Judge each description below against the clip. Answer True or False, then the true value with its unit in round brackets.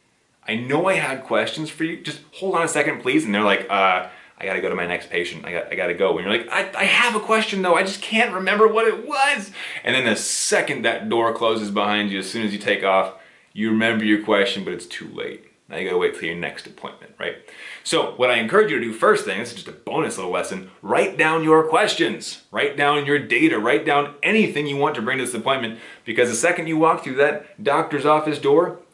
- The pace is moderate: False (250 wpm)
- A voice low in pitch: False (155 Hz)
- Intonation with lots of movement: True (7.9 semitones)